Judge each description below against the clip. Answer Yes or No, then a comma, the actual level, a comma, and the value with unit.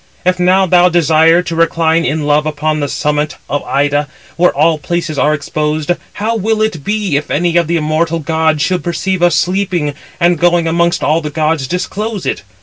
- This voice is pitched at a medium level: Yes, medium, 165 Hz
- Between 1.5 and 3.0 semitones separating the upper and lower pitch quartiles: Yes, average, 2.7 semitones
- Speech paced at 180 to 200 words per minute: Yes, average, 190 wpm